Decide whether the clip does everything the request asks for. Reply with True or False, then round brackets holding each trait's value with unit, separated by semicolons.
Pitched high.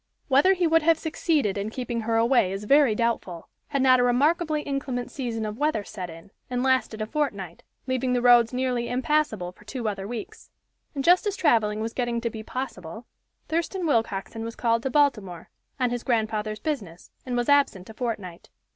True (240 Hz)